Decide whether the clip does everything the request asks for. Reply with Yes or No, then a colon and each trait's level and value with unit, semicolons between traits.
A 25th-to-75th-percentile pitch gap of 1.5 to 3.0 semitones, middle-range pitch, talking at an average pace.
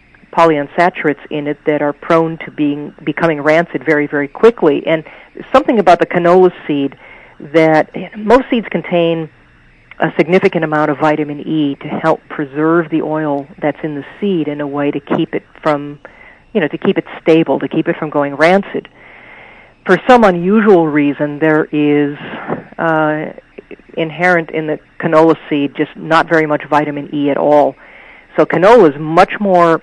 Yes: narrow, 2.6 semitones; medium, 155 Hz; average, 165 wpm